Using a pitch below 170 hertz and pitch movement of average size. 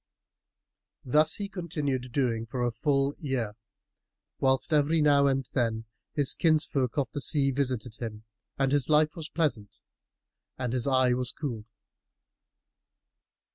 Yes: low, 135 Hz; average, 3.3 semitones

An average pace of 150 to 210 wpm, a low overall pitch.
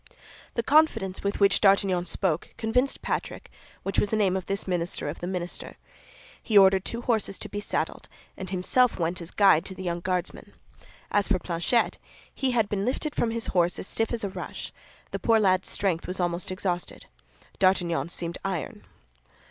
No: average, 180 wpm; high, 190 Hz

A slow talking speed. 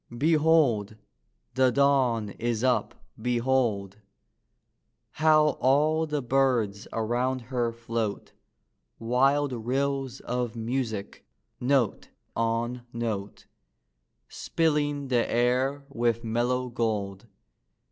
Yes: slow, 85 wpm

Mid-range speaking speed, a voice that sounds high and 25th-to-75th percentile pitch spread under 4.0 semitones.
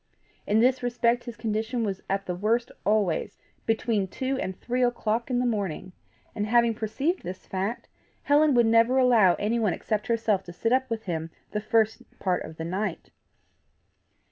Yes: average, 170 wpm; high, 220 Hz; average, 3.5 semitones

